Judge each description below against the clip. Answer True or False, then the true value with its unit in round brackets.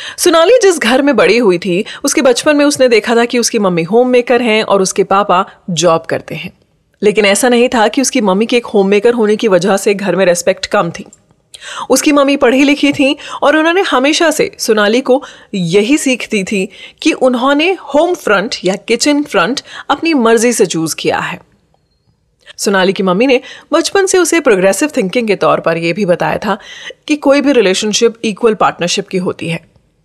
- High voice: True (235 Hz)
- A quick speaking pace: True (195 wpm)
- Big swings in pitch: True (6.5 semitones)